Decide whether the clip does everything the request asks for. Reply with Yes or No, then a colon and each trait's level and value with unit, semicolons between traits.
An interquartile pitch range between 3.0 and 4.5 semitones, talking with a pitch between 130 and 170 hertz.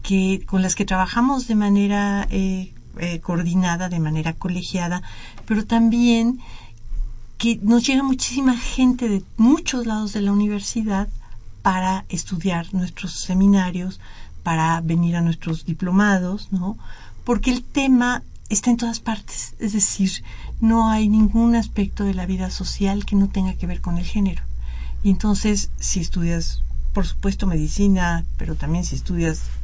No: average, 3.8 semitones; high, 190 Hz